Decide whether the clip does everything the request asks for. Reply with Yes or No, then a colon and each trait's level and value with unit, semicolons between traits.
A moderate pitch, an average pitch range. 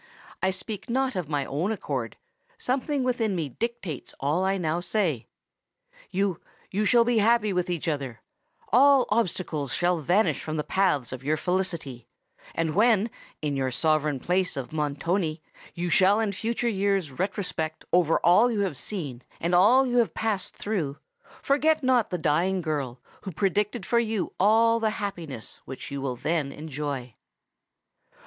No: medium, 180 Hz; wide, 6.2 semitones